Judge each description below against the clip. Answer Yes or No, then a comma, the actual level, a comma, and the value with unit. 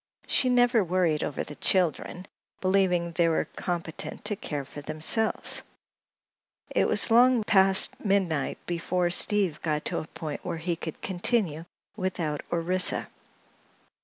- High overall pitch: No, medium, 175 Hz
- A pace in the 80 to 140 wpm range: Yes, slow, 135 wpm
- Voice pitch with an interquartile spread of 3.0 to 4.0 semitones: Yes, average, 3.4 semitones